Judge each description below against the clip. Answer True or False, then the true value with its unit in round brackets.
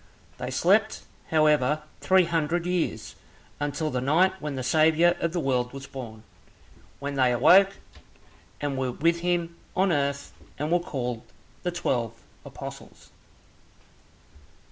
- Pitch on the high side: False (150 Hz)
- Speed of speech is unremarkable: False (130 wpm)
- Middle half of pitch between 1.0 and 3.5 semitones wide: False (4.7 semitones)